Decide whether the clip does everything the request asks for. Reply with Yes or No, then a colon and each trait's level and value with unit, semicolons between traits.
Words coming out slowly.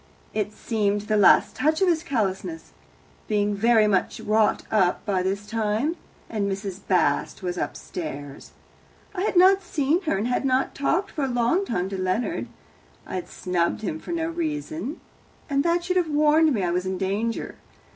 No: average, 175 wpm